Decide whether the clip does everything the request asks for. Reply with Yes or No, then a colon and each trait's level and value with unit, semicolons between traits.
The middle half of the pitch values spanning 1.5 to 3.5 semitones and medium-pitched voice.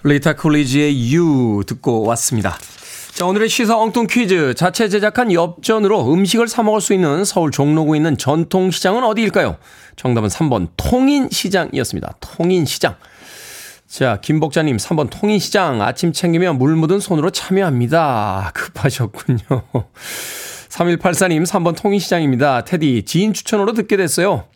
No: wide, 6.4 semitones; medium, 170 Hz